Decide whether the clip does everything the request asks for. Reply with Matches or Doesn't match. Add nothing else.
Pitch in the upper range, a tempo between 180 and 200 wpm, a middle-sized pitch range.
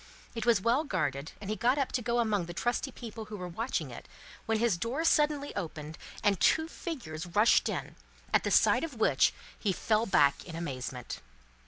Doesn't match